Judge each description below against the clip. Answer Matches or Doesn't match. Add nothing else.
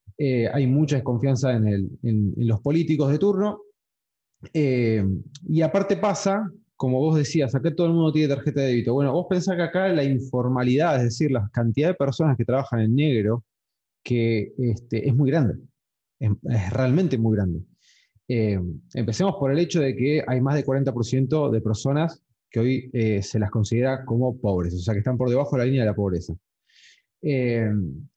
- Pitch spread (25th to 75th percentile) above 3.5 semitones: Matches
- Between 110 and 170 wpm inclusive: Doesn't match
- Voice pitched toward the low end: Matches